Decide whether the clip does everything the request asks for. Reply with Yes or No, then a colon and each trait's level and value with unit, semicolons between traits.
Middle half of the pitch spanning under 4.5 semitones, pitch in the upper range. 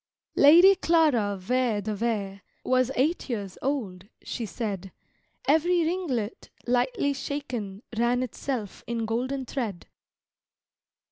No: average, 5.2 semitones; high, 245 Hz